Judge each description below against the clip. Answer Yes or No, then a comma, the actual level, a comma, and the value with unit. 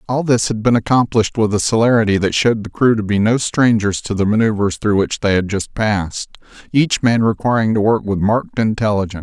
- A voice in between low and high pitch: No, low, 110 Hz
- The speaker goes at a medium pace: No, fast, 215 wpm